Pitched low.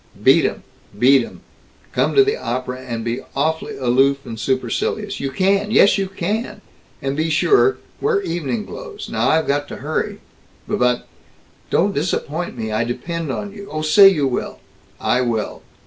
No: medium, 155 Hz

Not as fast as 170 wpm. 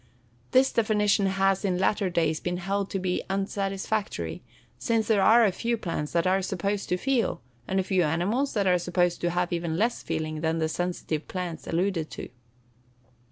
No: average, 180 wpm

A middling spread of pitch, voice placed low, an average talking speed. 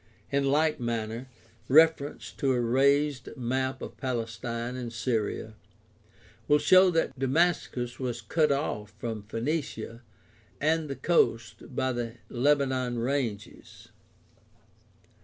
No: average, 3.5 semitones; low, 130 Hz; slow, 110 wpm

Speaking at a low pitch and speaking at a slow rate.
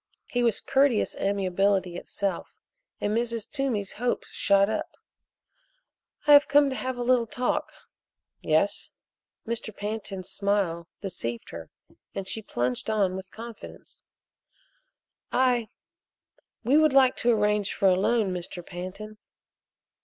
No: high, 210 Hz; slow, 125 wpm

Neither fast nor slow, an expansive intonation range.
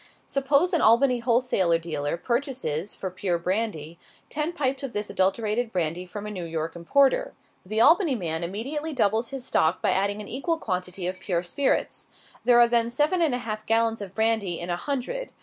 Yes: average, 185 wpm; wide, 6.4 semitones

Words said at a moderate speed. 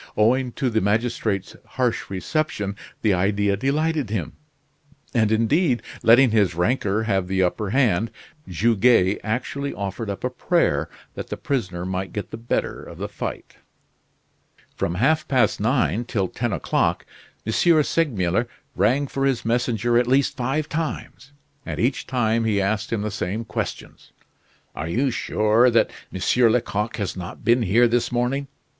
Yes: average, 150 wpm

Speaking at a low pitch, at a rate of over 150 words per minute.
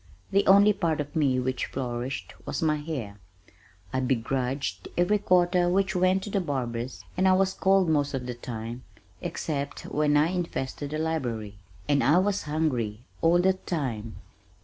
No: medium, 150 Hz; average, 165 wpm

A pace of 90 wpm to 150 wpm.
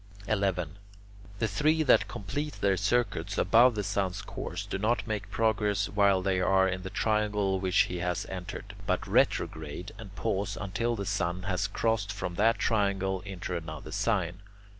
No: average, 160 wpm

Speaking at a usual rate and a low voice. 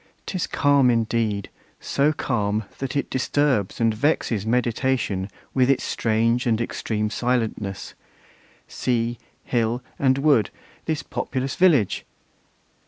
No: slow, 110 wpm; low, 120 Hz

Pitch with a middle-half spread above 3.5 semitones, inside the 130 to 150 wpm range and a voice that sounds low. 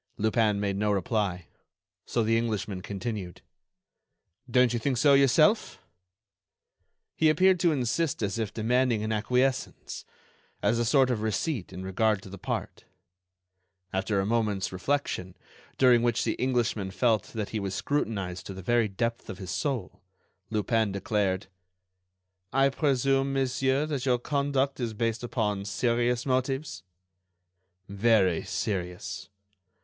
Yes: average, 4.6 semitones; slow, 135 wpm; low, 115 Hz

